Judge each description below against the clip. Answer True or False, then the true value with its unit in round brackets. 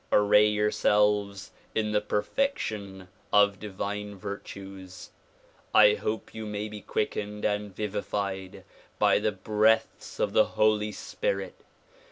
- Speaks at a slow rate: True (115 wpm)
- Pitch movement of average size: False (1.0 semitones)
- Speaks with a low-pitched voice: True (105 Hz)